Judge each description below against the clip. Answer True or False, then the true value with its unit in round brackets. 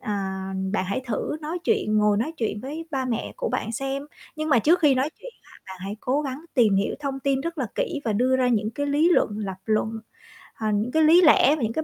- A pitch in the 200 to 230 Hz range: False (260 Hz)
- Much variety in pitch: True (5.9 semitones)